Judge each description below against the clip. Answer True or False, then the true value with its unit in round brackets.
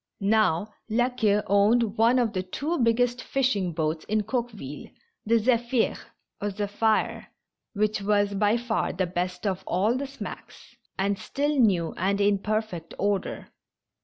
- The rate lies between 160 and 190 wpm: False (145 wpm)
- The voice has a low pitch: False (210 Hz)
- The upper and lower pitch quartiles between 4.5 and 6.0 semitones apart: False (3.3 semitones)